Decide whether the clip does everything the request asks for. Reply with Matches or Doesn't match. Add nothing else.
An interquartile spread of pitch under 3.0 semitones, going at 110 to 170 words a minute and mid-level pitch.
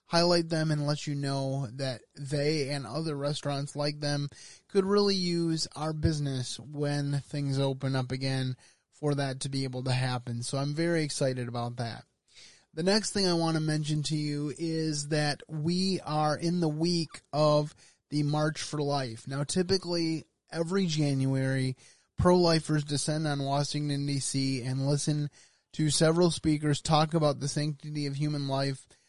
Matches